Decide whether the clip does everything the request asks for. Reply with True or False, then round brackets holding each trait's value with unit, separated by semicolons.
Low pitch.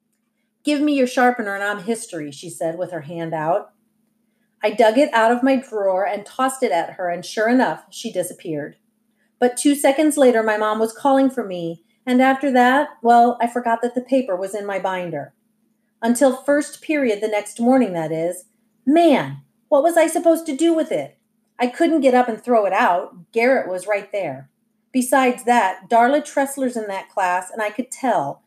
False (230 Hz)